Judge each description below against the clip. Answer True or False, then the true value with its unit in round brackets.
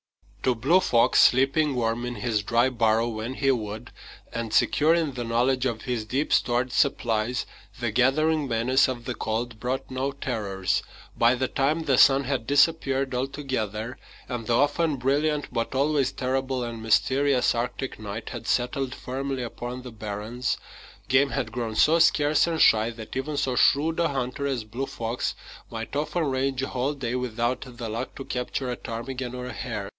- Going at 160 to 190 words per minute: True (175 wpm)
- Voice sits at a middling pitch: False (125 Hz)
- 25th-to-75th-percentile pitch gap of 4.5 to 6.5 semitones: False (2.8 semitones)